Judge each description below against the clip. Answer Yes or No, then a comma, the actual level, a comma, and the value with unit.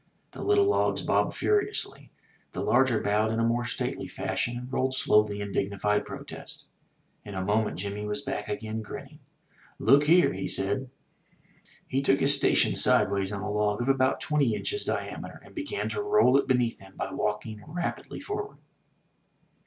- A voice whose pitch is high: No, low, 120 Hz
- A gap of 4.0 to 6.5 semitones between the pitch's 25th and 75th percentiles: Yes, average, 5.2 semitones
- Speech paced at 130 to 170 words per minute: Yes, average, 165 wpm